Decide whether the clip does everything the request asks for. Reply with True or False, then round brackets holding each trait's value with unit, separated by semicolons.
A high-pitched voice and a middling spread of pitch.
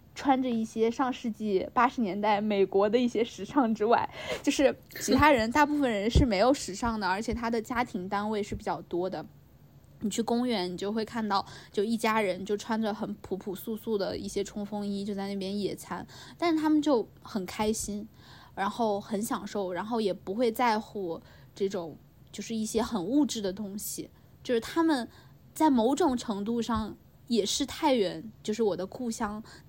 True (220 Hz; 3.0 semitones)